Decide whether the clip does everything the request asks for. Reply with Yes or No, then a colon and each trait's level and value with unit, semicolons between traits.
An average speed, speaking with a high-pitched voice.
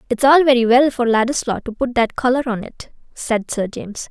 No: fast, 220 wpm; high, 245 Hz